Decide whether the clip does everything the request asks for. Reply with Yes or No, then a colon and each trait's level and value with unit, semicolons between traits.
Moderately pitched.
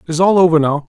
Yes: medium, 165 Hz